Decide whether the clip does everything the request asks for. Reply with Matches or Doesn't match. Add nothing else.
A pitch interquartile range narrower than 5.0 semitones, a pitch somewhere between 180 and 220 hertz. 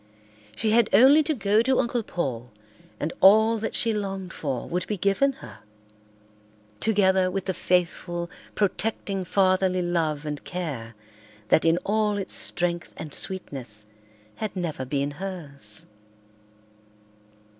Doesn't match